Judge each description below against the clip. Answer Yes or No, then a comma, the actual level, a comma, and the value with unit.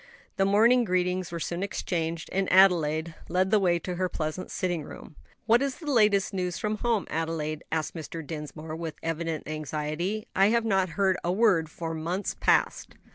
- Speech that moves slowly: No, average, 180 wpm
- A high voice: No, medium, 180 Hz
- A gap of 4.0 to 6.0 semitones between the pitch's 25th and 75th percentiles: No, average, 3.5 semitones